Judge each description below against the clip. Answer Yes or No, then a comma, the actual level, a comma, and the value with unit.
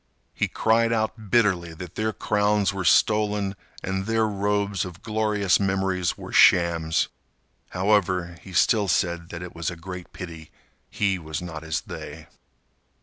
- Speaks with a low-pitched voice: Yes, very low, 95 Hz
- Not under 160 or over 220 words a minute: No, average, 145 wpm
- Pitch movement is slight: No, average, 3.3 semitones